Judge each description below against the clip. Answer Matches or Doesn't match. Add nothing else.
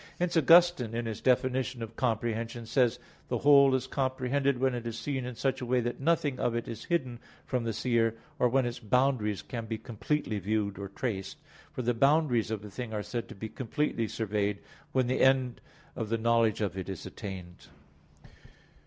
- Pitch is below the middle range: Matches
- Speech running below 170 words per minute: Doesn't match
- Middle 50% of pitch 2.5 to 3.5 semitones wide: Matches